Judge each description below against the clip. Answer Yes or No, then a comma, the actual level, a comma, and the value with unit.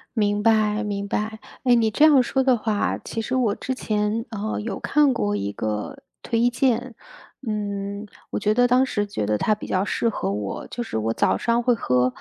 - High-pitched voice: Yes, high, 215 Hz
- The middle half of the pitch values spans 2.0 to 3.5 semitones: Yes, average, 3.1 semitones